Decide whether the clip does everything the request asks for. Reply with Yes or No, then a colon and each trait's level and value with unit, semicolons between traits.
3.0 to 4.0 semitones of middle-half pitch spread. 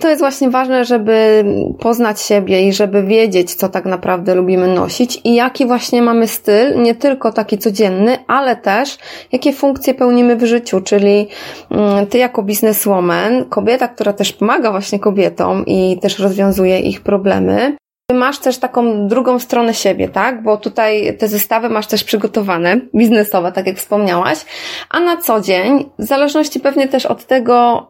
Yes: average, 3.7 semitones